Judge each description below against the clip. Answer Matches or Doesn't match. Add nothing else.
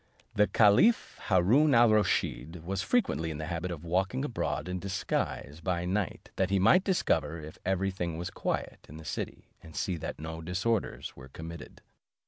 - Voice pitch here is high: Doesn't match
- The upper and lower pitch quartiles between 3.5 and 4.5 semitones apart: Matches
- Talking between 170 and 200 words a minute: Matches